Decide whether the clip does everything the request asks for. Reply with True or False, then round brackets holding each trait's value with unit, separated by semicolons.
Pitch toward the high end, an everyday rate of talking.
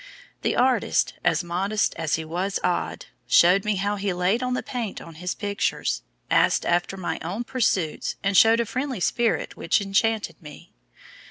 True (195 Hz; 170 wpm)